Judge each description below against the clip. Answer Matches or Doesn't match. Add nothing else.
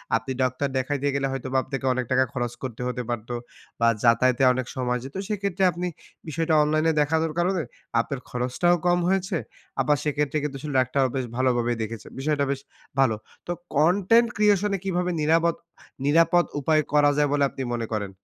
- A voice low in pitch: Doesn't match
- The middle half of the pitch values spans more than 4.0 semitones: Matches